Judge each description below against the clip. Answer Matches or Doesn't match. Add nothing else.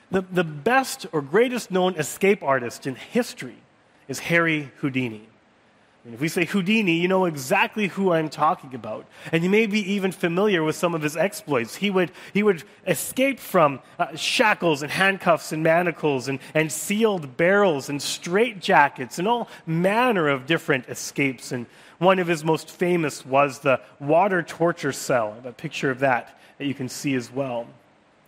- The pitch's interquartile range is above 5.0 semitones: Matches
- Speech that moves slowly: Doesn't match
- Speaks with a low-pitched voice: Doesn't match